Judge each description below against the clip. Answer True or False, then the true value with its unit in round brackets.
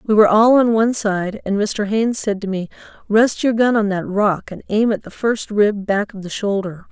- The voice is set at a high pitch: True (210 Hz)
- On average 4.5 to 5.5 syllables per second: True (5.1 syllables/s)